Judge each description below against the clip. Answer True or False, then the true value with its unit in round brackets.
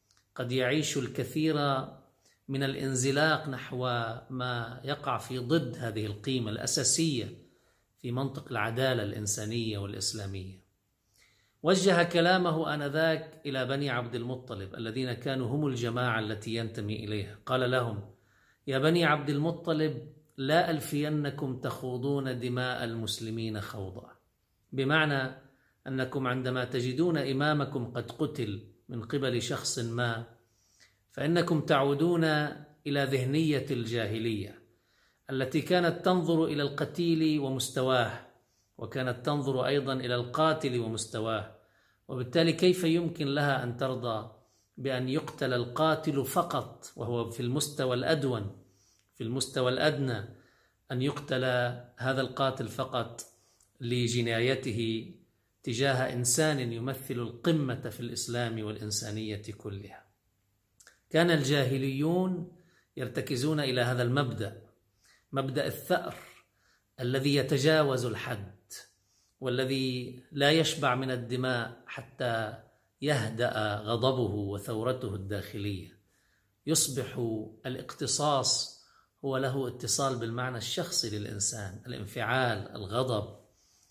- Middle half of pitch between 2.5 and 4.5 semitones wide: True (4.0 semitones)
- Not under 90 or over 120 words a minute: True (95 wpm)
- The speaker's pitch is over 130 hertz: False (125 Hz)